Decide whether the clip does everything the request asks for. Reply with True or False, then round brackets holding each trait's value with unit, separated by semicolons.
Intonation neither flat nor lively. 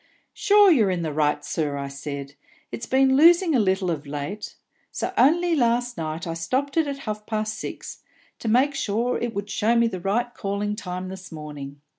False (7.3 semitones)